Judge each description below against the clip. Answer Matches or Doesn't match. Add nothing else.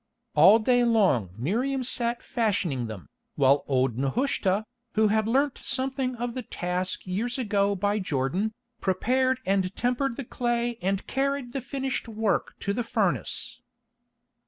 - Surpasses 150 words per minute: Doesn't match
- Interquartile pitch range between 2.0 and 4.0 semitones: Doesn't match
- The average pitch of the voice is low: Doesn't match